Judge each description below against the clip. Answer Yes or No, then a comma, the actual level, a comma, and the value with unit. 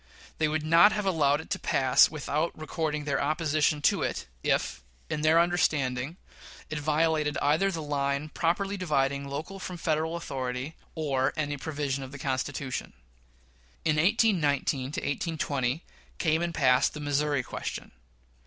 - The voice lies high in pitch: No, medium, 150 Hz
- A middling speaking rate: Yes, average, 145 wpm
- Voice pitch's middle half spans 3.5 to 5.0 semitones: No, narrow, 2.6 semitones